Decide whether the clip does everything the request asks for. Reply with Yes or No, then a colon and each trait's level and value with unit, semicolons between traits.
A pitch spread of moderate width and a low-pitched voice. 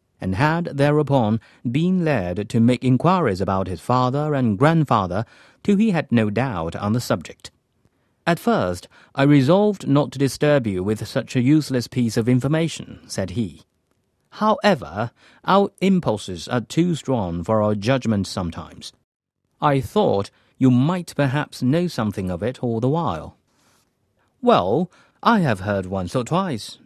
No: wide, 6.3 semitones; low, 125 Hz